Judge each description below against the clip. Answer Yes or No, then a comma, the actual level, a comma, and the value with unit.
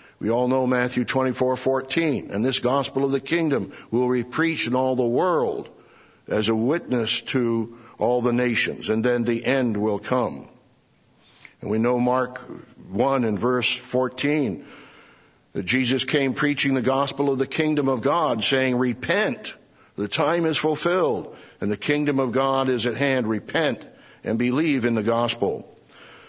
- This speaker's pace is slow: No, average, 160 wpm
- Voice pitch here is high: No, low, 125 Hz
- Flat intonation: Yes, narrow, 2.2 semitones